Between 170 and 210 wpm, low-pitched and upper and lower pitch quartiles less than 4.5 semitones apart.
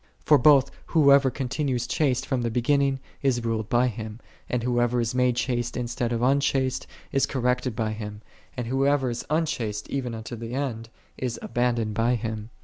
Yes: average, 175 wpm; low, 125 Hz; average, 2.7 semitones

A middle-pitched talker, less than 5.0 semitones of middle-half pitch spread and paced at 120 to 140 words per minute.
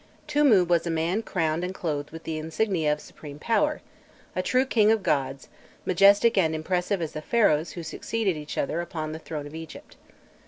No: medium, 170 Hz; average, 4.4 semitones; average, 190 wpm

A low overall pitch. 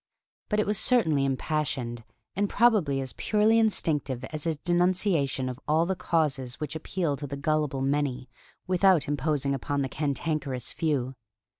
No: medium, 150 Hz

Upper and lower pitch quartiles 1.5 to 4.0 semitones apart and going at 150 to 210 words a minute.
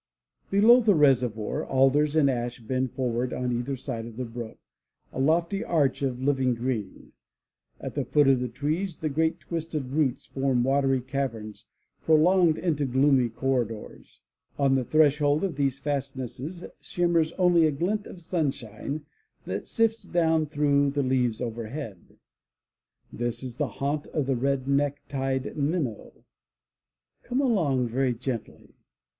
No: average, 3.7 semitones; average, 140 wpm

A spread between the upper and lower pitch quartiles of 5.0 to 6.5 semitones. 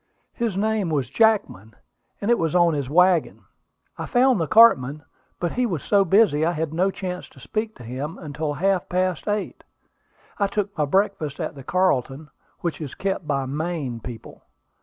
Yes: average, 5.3 semitones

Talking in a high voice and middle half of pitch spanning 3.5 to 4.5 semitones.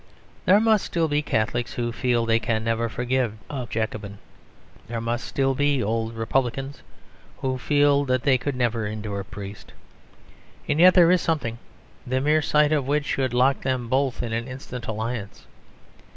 No: low, 125 Hz; average, 3.8 semitones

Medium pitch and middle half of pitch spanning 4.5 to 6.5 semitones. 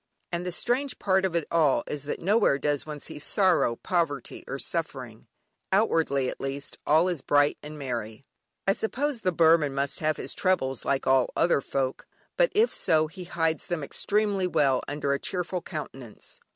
Yes: medium, 155 Hz; average, 4.8 semitones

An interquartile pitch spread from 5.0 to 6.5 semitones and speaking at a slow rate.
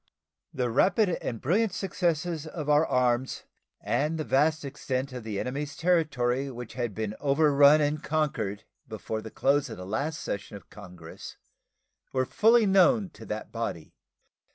No: wide, 5.4 semitones; average, 155 wpm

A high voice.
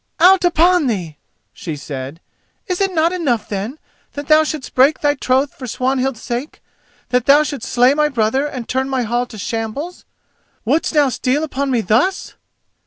Yes: very high, 265 Hz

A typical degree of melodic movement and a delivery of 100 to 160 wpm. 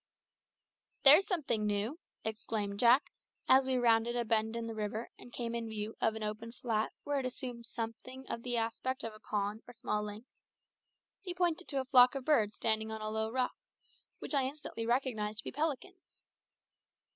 No: average, 3.1 semitones; average, 180 wpm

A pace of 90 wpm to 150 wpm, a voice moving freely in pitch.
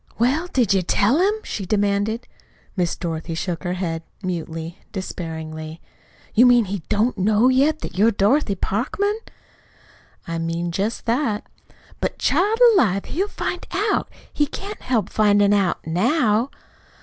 Yes: average, 140 wpm; wide, 6.1 semitones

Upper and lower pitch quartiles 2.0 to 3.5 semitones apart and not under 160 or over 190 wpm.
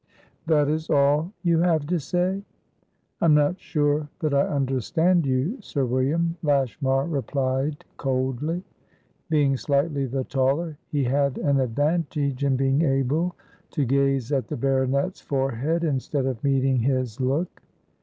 No: average, 2.9 semitones; average, 140 wpm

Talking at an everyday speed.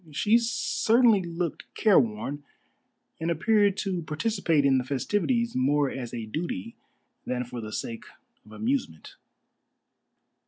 No: slow, 120 wpm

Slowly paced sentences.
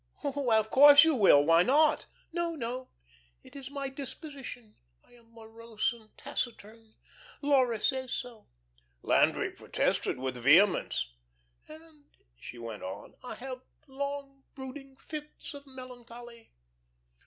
Yes: slow, 125 wpm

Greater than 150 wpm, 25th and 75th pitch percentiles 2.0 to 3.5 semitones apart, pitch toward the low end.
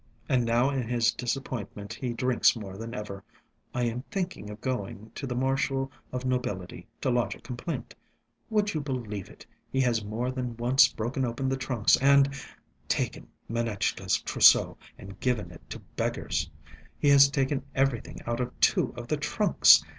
Yes: average, 170 wpm; average, 3.0 semitones; low, 125 Hz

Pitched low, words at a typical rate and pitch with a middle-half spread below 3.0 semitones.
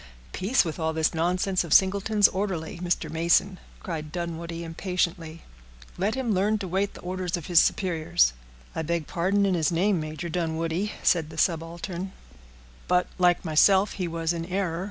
No: medium, 175 Hz; average, 165 wpm; narrow, 2.5 semitones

